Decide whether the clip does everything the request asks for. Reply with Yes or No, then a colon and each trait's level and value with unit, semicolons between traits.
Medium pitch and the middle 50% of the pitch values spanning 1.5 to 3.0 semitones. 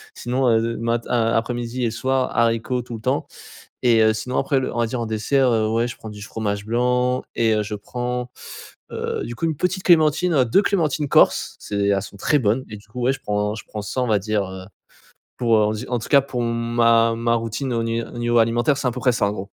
No: low, 115 Hz; narrow, 2.4 semitones